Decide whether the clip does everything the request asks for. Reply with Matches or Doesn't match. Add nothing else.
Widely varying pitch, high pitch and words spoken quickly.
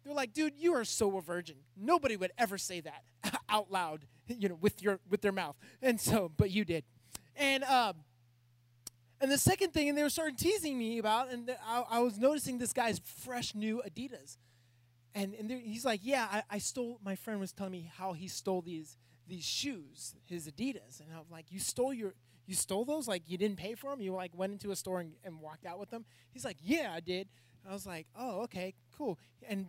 Matches